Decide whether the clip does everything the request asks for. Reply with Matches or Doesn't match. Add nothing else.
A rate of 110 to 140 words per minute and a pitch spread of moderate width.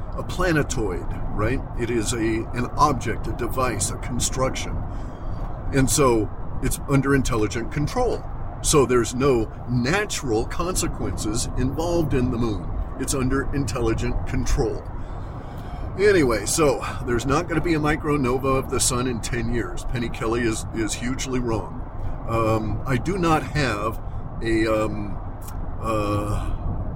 Matches